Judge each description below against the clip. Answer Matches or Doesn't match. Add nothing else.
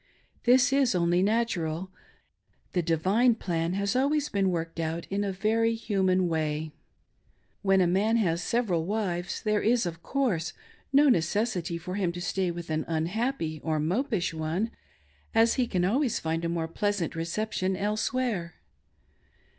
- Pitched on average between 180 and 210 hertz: Matches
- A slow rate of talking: Doesn't match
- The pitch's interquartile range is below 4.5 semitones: Doesn't match